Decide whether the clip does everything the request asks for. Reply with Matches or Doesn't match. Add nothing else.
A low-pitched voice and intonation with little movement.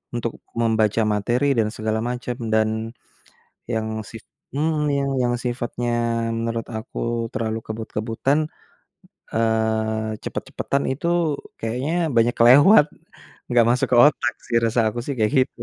Matches